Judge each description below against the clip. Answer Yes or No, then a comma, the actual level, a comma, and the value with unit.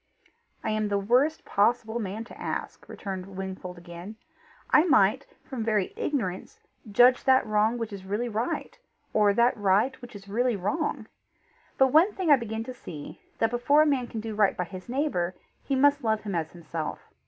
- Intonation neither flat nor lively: Yes, average, 4.5 semitones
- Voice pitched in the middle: No, high, 220 Hz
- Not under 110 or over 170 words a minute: No, average, 185 wpm